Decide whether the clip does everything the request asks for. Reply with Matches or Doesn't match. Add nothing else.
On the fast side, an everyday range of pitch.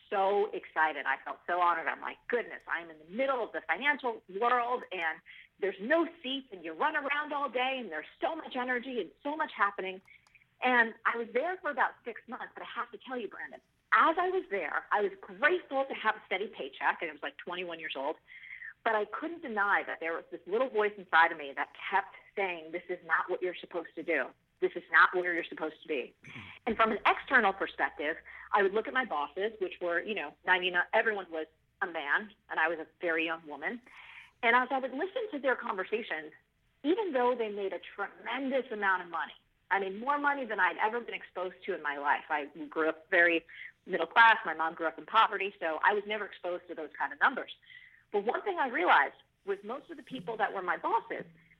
Doesn't match